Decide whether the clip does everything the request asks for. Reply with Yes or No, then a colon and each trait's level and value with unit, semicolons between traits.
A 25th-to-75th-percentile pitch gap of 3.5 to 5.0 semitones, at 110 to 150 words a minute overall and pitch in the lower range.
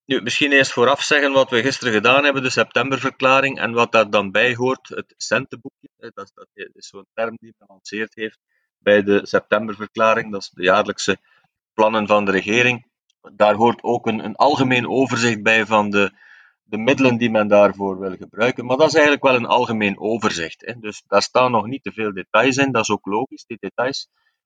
No: average, 4.0 semitones; fast, 200 wpm; low, 115 Hz